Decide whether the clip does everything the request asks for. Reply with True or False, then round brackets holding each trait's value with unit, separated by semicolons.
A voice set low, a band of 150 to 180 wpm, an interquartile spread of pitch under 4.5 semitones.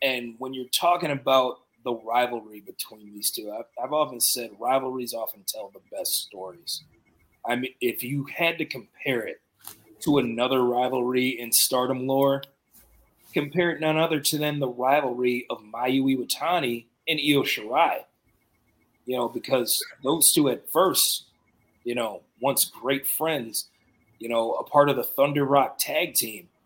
True (130 Hz; 160 wpm; 2.6 semitones)